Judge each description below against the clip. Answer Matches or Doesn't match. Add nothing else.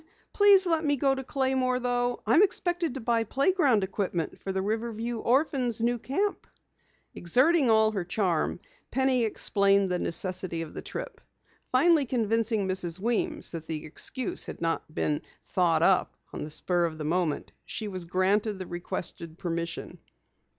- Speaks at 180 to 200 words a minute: Doesn't match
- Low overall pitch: Doesn't match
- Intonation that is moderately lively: Doesn't match